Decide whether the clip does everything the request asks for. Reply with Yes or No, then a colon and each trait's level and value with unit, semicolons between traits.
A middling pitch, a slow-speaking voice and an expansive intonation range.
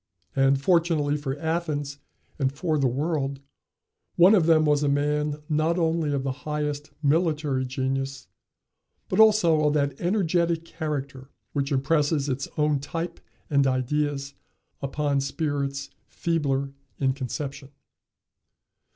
No: medium, 145 Hz; slow, 125 wpm; narrow, 2.6 semitones